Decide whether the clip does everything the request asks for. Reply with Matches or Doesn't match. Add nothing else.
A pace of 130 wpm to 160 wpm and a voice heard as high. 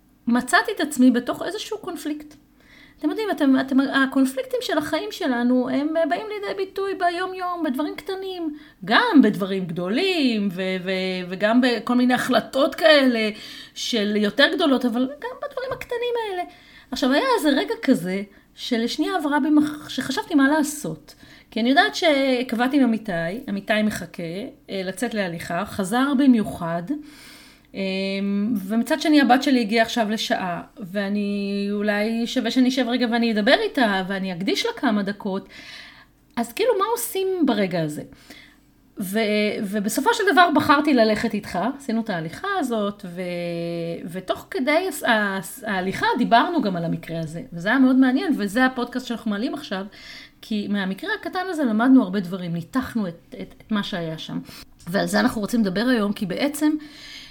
Matches